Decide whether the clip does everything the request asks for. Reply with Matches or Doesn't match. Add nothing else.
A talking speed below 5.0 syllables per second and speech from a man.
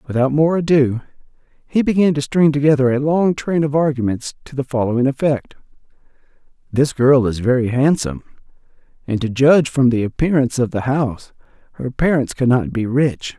Doesn't match